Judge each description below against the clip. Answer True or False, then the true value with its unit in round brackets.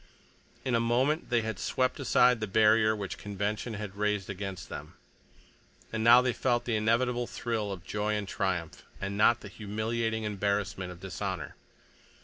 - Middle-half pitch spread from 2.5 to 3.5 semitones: True (2.8 semitones)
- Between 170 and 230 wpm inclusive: False (160 wpm)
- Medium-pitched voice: False (105 Hz)